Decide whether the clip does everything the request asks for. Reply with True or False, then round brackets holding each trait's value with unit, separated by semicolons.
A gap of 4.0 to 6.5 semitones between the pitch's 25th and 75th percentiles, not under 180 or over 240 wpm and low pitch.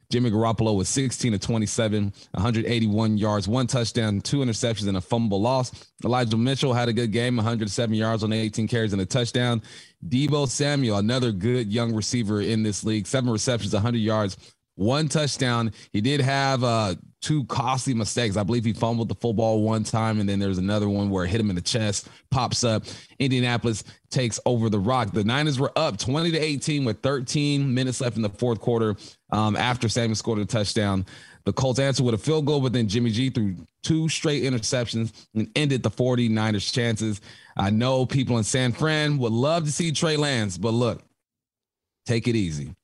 False (3.2 semitones; 190 wpm; 115 Hz)